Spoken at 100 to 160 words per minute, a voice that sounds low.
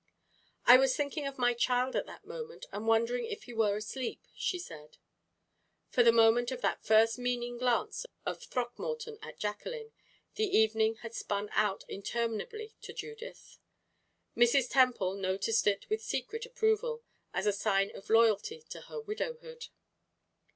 No: average, 150 wpm; high, 245 Hz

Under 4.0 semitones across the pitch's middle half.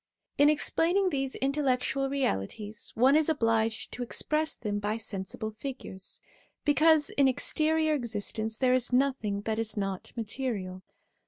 No: average, 4.7 semitones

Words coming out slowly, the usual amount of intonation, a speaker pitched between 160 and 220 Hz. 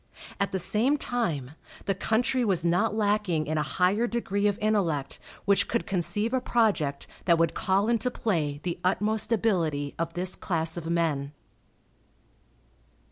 No: average, 150 wpm; average, 4.8 semitones; high, 190 Hz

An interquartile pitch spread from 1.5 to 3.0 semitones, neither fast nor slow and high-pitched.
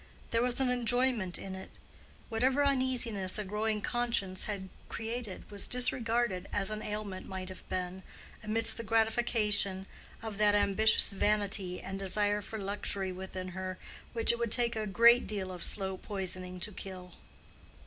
No: average, 3.4 semitones; average, 155 wpm; high, 210 Hz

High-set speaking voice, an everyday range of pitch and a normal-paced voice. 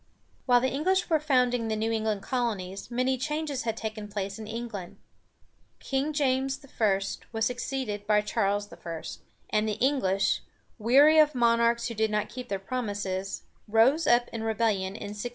Yes: high, 225 Hz; average, 3.8 semitones; average, 165 wpm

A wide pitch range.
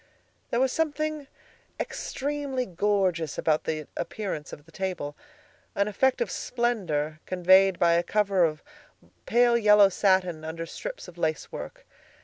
Yes: wide, 6.4 semitones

